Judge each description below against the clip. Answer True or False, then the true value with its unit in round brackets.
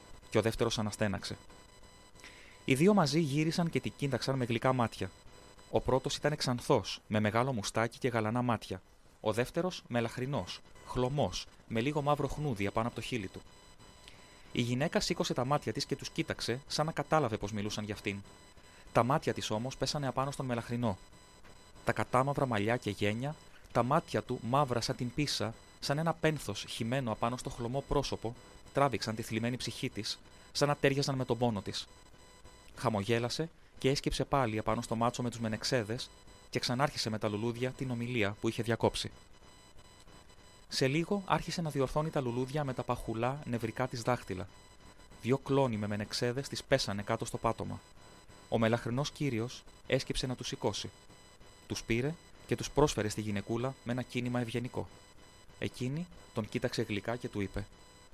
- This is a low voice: True (115 Hz)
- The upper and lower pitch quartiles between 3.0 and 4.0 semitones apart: False (4.9 semitones)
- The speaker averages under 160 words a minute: False (165 wpm)